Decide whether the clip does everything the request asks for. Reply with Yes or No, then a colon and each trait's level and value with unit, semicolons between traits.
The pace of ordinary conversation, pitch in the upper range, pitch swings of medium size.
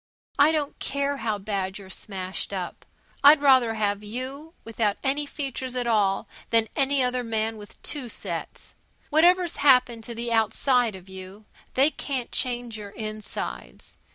Yes: average, 155 wpm; high, 235 Hz; average, 4.7 semitones